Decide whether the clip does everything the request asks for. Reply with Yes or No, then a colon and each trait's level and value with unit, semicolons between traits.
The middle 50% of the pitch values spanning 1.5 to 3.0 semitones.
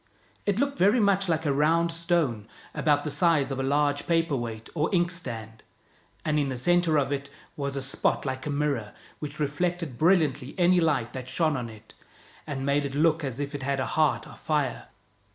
No: average, 3.7 semitones